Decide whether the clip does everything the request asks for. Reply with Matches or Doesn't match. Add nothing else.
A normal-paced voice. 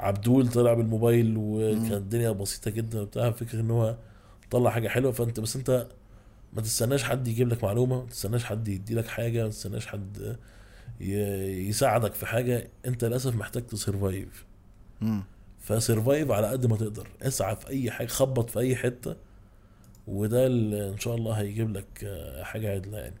Doesn't match